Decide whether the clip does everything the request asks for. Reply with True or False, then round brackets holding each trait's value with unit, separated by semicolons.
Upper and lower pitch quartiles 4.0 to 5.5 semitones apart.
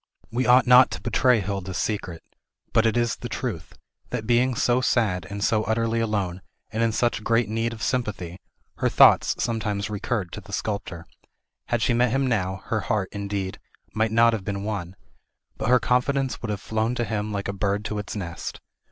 False (2.9 semitones)